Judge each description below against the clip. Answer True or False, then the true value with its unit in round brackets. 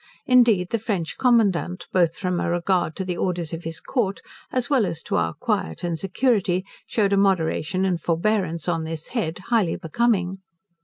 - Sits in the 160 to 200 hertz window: True (185 Hz)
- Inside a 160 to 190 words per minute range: True (175 wpm)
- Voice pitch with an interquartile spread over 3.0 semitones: True (4.1 semitones)